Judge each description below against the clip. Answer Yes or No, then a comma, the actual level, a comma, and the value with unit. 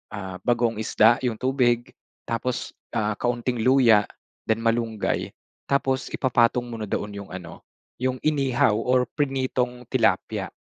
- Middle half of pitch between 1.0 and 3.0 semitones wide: Yes, average, 2.7 semitones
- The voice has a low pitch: Yes, low, 120 Hz